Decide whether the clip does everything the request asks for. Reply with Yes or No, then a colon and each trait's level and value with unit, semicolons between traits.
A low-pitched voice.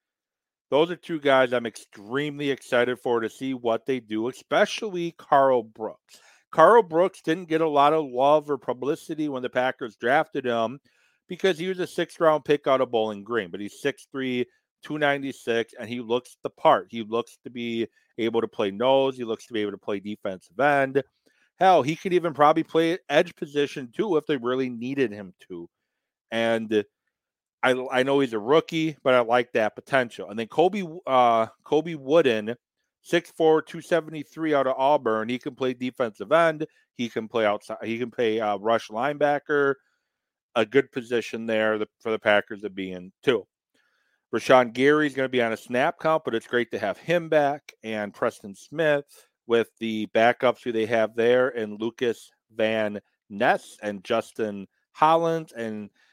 Yes: low, 130 Hz